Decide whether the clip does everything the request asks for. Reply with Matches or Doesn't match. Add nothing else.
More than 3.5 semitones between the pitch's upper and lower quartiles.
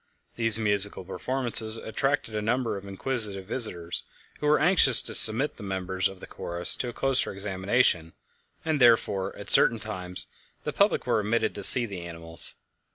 Matches